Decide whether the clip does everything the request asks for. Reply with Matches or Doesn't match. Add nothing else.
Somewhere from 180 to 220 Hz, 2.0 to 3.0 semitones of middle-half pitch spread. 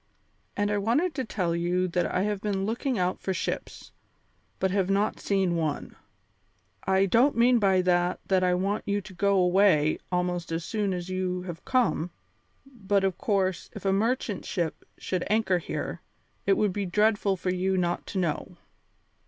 Matches